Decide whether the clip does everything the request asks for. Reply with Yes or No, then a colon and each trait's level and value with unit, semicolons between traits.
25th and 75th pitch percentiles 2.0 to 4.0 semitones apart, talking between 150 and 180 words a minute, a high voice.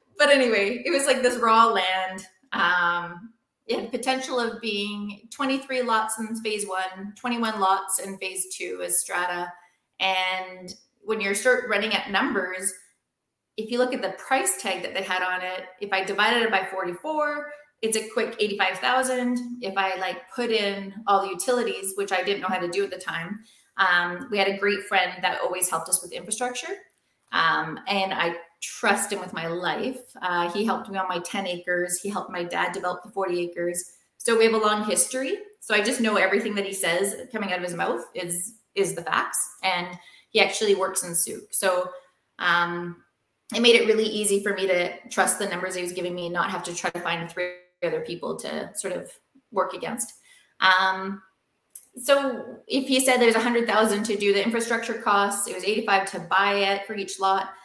No: average, 3.7 semitones; average, 200 wpm; high, 195 Hz